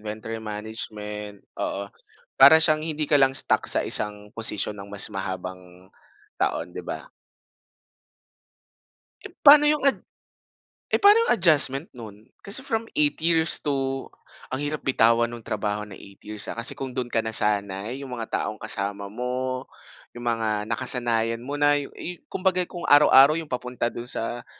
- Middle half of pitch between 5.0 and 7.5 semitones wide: Yes, wide, 5.6 semitones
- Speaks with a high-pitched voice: No, low, 120 Hz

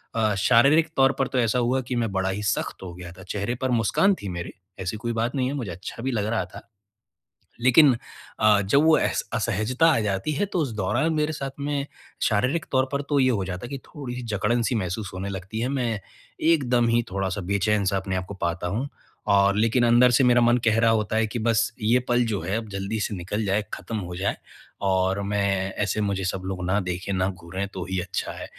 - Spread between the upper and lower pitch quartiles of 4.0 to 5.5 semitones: Yes, average, 4.3 semitones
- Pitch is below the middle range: Yes, low, 110 Hz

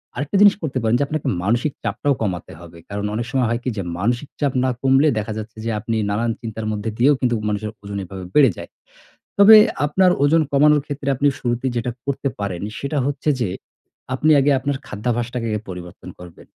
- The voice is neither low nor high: No, low, 120 Hz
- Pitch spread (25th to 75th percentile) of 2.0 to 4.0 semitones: No, average, 5.0 semitones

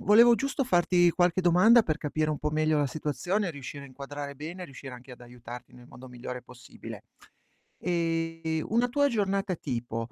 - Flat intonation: No, wide, 5.5 semitones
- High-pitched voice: No, medium, 155 Hz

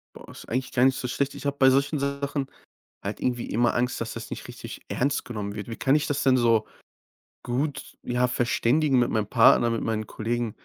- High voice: No, low, 125 Hz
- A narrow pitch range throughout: No, average, 3.0 semitones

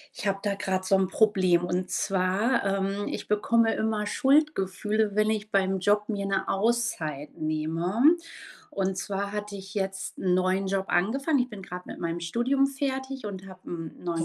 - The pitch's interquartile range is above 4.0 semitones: No, average, 2.8 semitones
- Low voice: No, high, 195 Hz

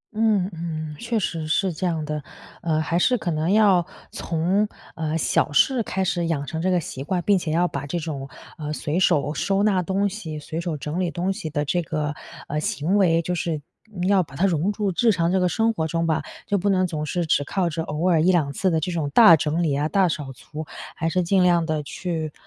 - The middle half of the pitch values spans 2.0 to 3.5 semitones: Yes, average, 3.2 semitones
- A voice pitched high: No, medium, 170 Hz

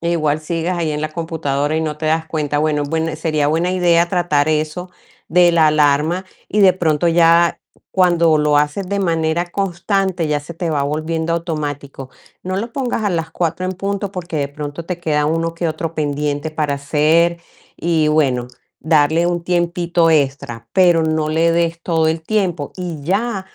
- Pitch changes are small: Yes, narrow, 2.3 semitones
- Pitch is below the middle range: No, medium, 165 Hz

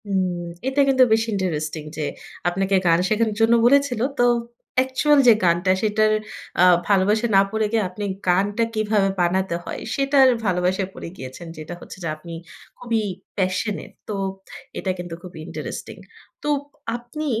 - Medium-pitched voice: No, high, 205 Hz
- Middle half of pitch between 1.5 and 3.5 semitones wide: No, average, 4.5 semitones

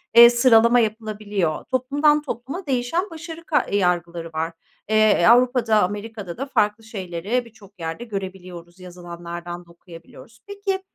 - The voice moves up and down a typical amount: No, wide, 6.0 semitones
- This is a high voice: Yes, high, 215 Hz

